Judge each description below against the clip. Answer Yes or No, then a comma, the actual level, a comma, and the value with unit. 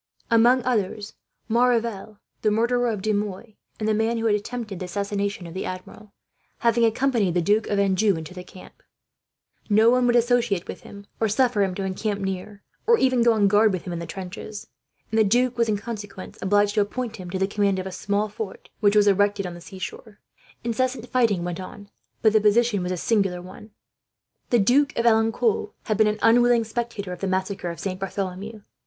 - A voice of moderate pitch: No, high, 210 Hz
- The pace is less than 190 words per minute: No, fast, 205 wpm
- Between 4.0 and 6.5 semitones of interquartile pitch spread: No, average, 3.1 semitones